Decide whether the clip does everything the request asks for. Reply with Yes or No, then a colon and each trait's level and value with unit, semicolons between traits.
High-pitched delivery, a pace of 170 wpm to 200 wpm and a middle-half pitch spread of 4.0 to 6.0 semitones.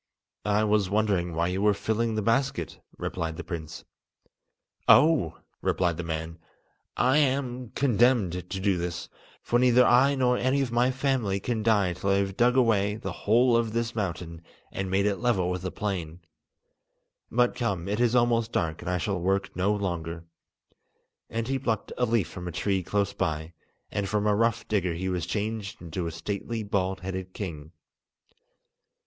No: low, 100 Hz; average, 175 wpm; average, 4.6 semitones